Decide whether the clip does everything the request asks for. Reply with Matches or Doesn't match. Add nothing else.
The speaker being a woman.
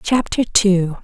Matches